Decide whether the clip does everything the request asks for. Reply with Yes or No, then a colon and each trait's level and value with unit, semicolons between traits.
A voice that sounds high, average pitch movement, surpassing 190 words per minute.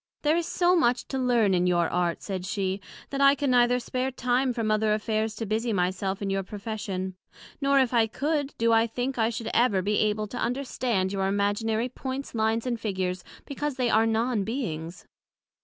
Yes: high, 225 Hz; average, 4.1 semitones; average, 200 wpm